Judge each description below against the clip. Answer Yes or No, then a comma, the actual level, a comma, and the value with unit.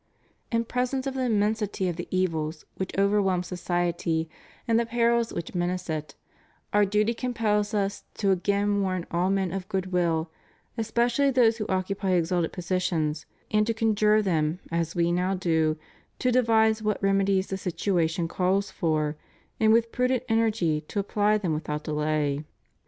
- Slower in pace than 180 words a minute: Yes, average, 160 wpm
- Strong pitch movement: No, average, 4.2 semitones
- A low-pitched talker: No, high, 195 Hz